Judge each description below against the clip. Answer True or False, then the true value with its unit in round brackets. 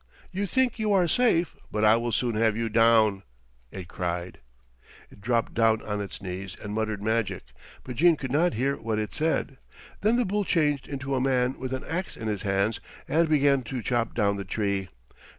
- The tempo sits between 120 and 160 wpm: False (200 wpm)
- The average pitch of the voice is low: True (115 Hz)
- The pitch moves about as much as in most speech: False (5.8 semitones)